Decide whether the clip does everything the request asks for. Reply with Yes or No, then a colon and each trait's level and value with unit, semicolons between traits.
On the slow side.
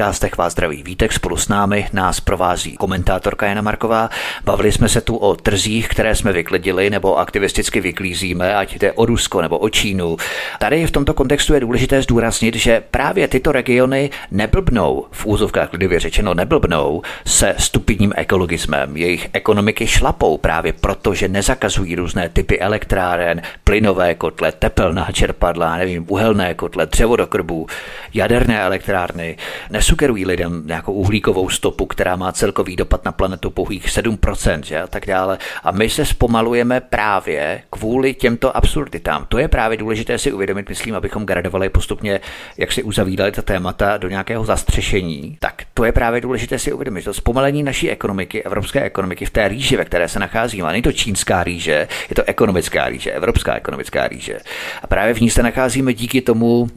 No: average, 165 wpm